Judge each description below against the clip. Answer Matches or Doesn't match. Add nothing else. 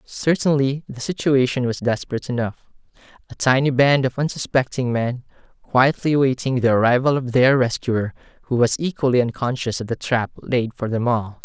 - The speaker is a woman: Doesn't match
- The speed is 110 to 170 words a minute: Matches